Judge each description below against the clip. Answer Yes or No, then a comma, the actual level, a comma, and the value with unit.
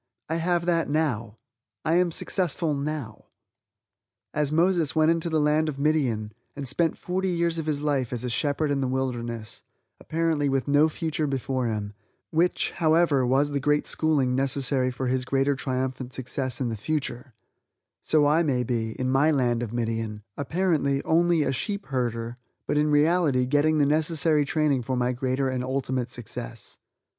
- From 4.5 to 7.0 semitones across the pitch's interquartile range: No, average, 3.8 semitones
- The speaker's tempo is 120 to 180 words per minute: Yes, average, 170 wpm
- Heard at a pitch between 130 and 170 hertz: Yes, medium, 140 Hz